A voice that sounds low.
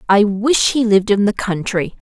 No: high, 210 Hz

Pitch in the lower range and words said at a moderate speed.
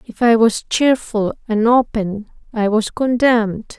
No: high, 225 Hz; average, 145 wpm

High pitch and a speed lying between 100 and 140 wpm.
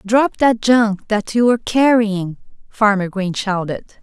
Yes: high, 215 Hz; slow, 135 wpm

